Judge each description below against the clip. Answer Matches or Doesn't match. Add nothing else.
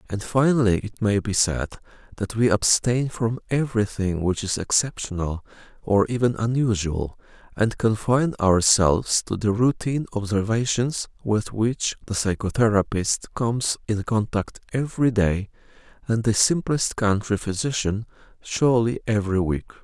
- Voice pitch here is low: Matches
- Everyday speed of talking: Doesn't match